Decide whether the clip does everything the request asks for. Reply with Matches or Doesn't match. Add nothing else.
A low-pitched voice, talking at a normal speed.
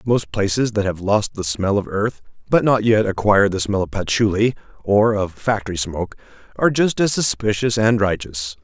Matches